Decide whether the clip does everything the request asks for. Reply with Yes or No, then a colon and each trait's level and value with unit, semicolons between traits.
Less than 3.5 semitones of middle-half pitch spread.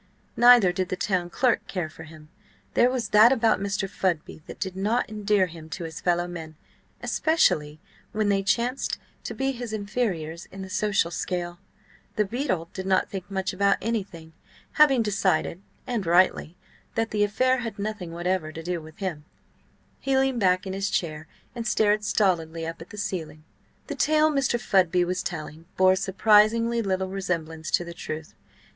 No: average, 4.1 semitones